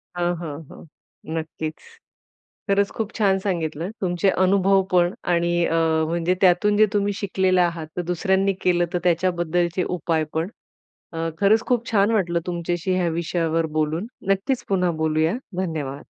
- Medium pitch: Yes, medium, 175 Hz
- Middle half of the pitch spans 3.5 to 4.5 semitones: No, average, 2.8 semitones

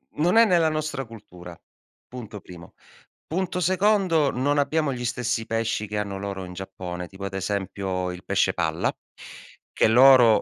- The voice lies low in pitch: Yes, low, 115 Hz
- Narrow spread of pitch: No, wide, 7.9 semitones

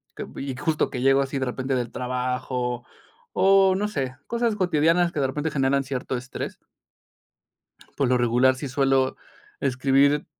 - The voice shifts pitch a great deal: No, average, 2.7 semitones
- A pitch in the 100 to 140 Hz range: Yes, low, 135 Hz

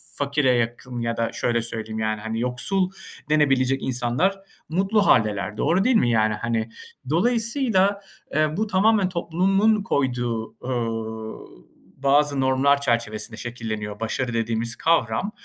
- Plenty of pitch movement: Yes, wide, 7.7 semitones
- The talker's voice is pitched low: Yes, low, 125 Hz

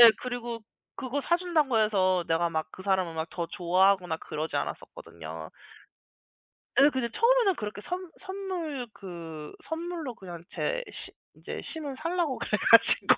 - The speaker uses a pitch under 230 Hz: No, high, 235 Hz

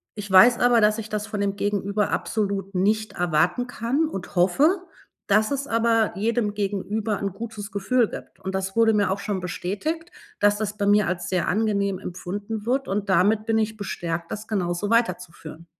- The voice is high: Yes, high, 205 Hz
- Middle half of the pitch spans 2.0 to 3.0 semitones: Yes, narrow, 2.6 semitones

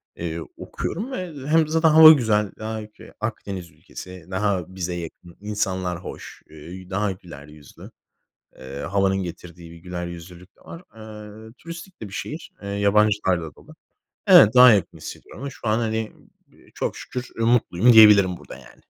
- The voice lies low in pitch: Yes, low, 100 Hz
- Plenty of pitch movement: No, average, 4.1 semitones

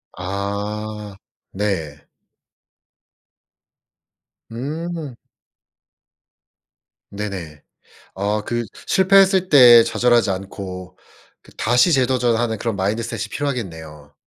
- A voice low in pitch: Yes, low, 105 Hz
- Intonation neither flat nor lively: Yes, average, 4.4 semitones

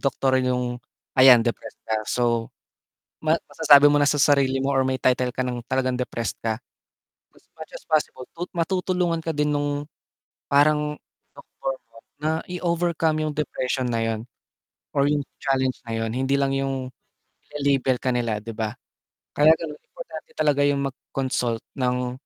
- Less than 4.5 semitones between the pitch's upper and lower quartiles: Yes, average, 3.0 semitones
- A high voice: No, low, 135 Hz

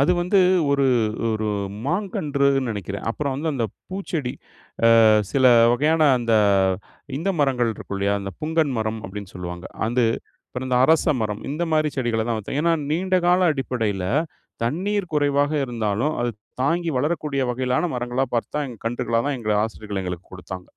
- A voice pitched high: No, low, 130 Hz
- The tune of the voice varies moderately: No, wide, 5.7 semitones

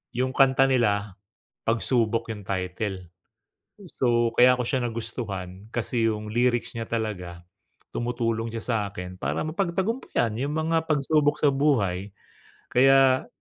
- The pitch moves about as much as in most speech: Yes, average, 4.2 semitones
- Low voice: Yes, low, 120 Hz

